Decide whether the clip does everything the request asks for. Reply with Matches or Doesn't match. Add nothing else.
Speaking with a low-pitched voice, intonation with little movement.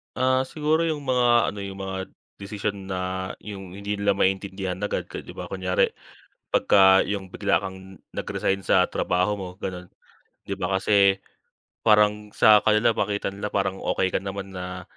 Matches